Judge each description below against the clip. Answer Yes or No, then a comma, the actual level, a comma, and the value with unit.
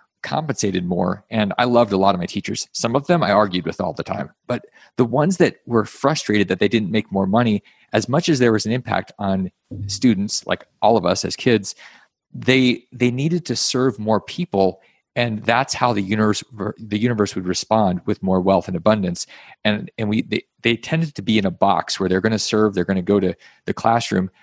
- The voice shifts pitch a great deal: No, average, 4.0 semitones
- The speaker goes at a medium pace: No, fast, 220 wpm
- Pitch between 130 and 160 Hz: No, low, 110 Hz